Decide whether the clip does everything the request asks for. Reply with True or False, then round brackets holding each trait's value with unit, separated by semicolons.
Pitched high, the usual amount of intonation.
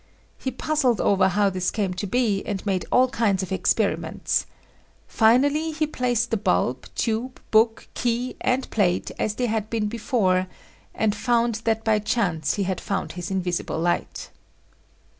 True (215 Hz; 4.1 semitones)